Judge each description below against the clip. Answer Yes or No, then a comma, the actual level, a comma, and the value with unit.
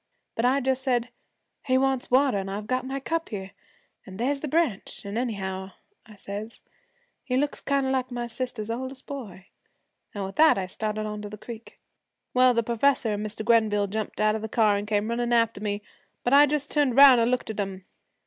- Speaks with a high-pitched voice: Yes, high, 230 Hz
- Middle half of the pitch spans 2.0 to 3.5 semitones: No, average, 4.0 semitones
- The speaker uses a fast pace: Yes, fast, 210 wpm